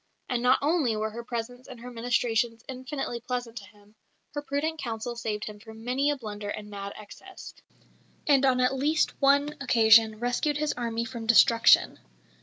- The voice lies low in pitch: No, high, 240 Hz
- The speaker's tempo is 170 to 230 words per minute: Yes, average, 175 wpm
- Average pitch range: Yes, average, 3.2 semitones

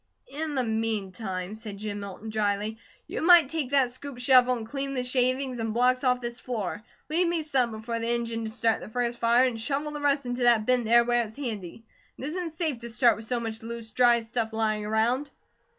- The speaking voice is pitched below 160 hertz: No, high, 235 Hz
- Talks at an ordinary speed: No, fast, 215 wpm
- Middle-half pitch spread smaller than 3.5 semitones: Yes, average, 2.7 semitones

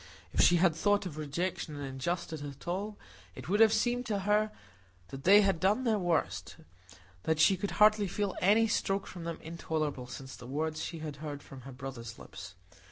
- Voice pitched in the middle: Yes, medium, 170 Hz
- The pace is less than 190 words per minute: No, average, 195 wpm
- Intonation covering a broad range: Yes, wide, 6.0 semitones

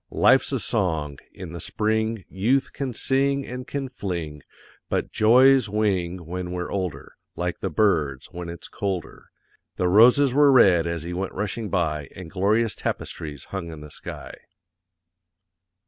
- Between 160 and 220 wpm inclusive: No, average, 150 wpm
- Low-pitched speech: Yes, very low, 95 Hz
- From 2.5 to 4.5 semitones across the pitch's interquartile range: No, average, 5.0 semitones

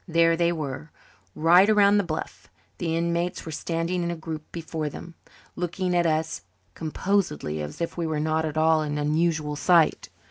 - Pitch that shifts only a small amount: Yes, narrow, 1.8 semitones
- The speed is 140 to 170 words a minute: No, average, 180 wpm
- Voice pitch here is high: No, medium, 165 Hz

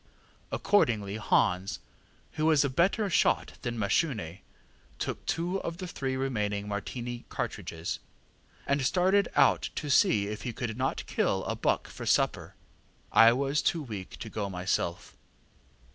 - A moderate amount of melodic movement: No, wide, 6.5 semitones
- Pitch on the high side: No, low, 120 Hz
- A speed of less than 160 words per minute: Yes, average, 145 wpm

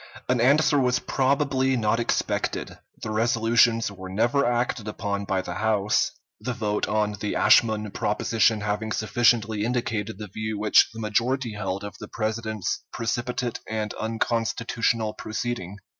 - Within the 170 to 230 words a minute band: No, average, 140 wpm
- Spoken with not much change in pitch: Yes, narrow, 2.2 semitones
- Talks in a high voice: No, low, 110 Hz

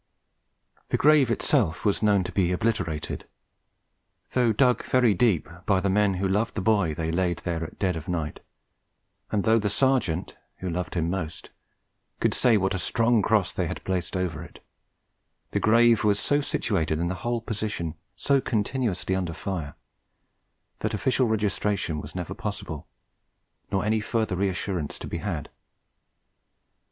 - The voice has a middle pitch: No, low, 100 Hz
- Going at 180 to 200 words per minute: No, average, 155 wpm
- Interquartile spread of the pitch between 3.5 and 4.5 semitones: Yes, average, 4.2 semitones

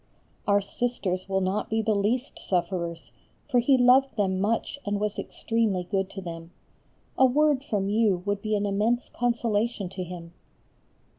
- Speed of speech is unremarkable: Yes, average, 160 wpm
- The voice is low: No, high, 205 Hz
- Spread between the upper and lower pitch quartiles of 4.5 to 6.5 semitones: No, average, 3.8 semitones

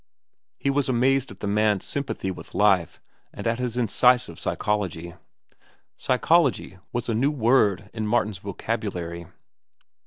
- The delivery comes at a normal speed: No, slow, 130 wpm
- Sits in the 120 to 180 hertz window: No, low, 110 Hz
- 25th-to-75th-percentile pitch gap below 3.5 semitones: No, average, 4.4 semitones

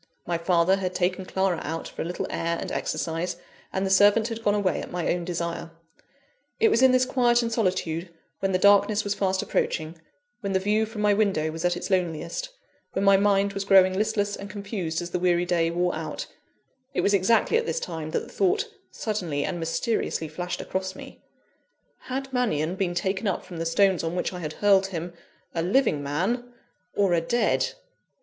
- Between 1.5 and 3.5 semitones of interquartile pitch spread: Yes, average, 3.2 semitones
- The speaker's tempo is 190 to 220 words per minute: Yes, average, 200 wpm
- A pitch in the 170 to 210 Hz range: Yes, high, 190 Hz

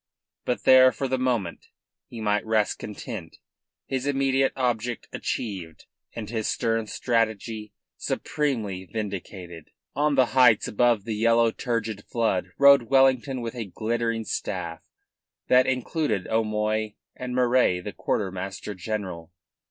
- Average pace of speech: No, slow, 125 wpm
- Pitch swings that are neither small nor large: Yes, average, 3.3 semitones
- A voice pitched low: Yes, low, 115 Hz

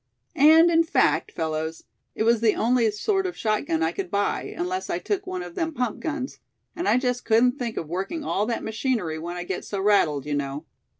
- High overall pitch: Yes, high, 220 Hz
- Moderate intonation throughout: No, wide, 8.1 semitones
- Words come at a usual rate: No, fast, 215 wpm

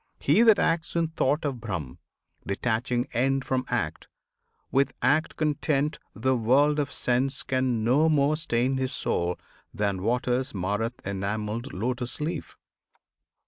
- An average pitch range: Yes, average, 4.2 semitones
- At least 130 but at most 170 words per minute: Yes, average, 140 wpm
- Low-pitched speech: Yes, low, 130 Hz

